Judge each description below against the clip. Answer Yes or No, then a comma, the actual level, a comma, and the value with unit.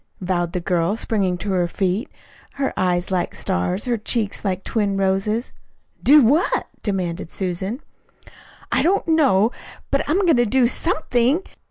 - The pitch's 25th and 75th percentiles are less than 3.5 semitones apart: No, wide, 5.6 semitones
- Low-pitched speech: No, high, 205 Hz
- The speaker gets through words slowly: No, average, 150 wpm